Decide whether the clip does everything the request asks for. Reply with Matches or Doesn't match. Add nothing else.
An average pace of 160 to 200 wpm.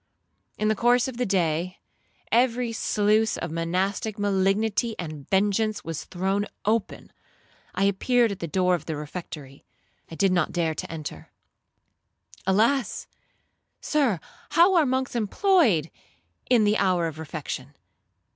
Doesn't match